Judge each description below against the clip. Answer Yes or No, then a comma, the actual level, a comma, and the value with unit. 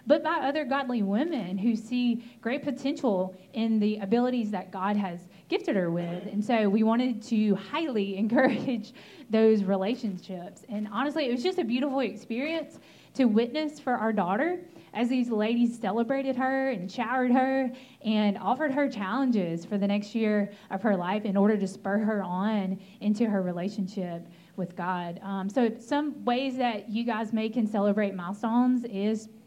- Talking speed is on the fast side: No, average, 165 wpm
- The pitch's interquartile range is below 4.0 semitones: No, average, 4.3 semitones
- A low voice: No, high, 220 Hz